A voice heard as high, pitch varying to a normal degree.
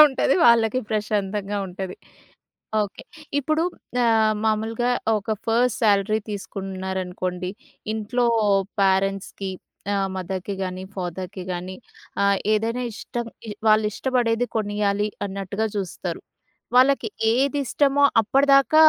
Yes: high, 210 Hz; average, 3.6 semitones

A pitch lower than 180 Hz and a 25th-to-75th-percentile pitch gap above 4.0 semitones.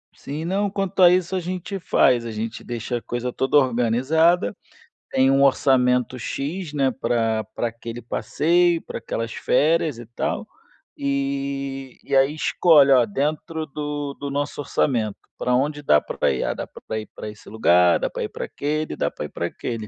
Yes: low, 135 Hz; average, 4.4 semitones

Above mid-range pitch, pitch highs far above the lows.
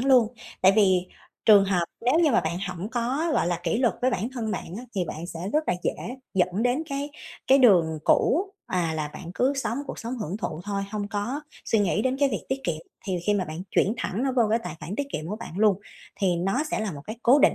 Yes: high, 210 Hz; wide, 5.7 semitones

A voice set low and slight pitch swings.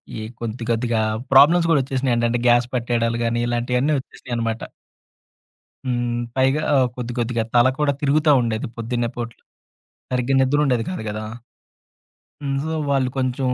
Yes: low, 125 Hz; narrow, 2.2 semitones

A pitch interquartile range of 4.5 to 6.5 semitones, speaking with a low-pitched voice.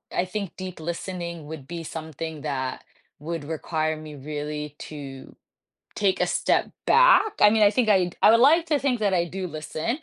No: average, 4.8 semitones; medium, 170 Hz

